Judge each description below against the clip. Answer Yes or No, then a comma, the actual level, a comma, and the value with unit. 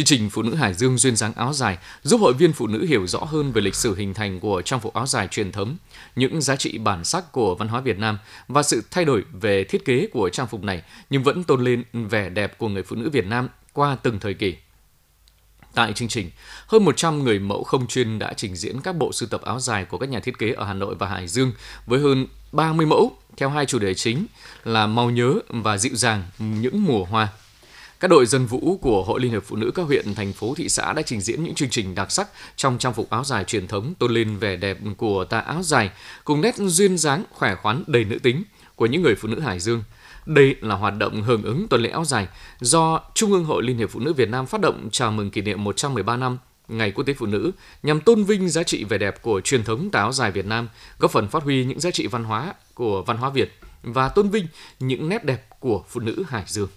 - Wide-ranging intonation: No, average, 4.7 semitones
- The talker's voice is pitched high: No, low, 115 Hz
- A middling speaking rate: No, fast, 255 wpm